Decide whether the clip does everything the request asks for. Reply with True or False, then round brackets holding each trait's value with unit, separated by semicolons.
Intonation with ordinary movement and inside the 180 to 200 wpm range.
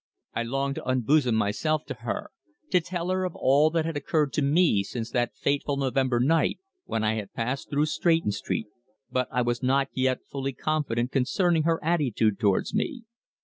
True (4.6 semitones; 185 wpm)